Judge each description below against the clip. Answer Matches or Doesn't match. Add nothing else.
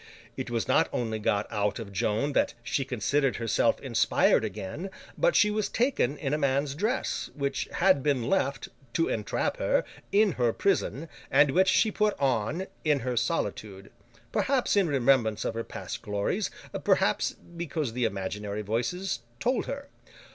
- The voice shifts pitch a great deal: Matches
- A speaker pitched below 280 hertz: Matches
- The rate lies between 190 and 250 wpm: Doesn't match